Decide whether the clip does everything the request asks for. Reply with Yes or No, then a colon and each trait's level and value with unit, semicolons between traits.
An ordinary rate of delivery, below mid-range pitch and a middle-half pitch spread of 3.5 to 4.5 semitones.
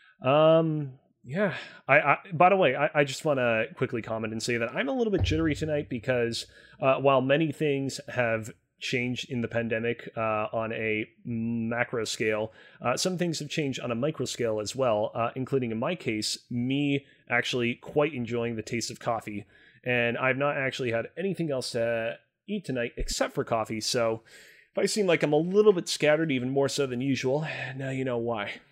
Yes: average, 195 wpm; low, 130 Hz; average, 4.0 semitones